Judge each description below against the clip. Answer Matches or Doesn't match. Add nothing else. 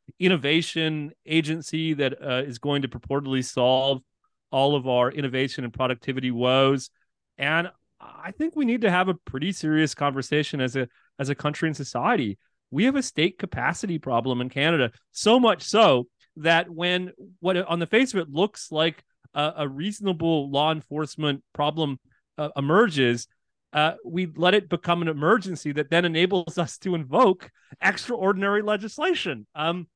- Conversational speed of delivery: Matches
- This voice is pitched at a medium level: Matches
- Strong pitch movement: Doesn't match